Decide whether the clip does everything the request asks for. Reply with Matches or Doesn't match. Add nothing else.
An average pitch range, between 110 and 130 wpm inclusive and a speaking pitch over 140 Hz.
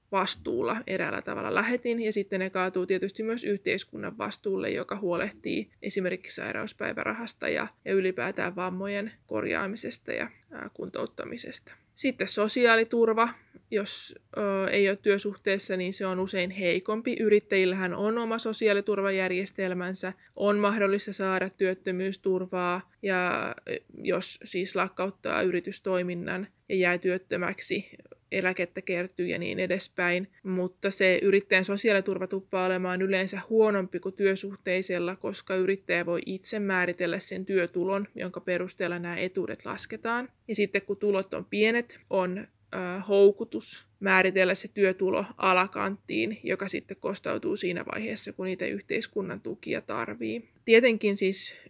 Doesn't match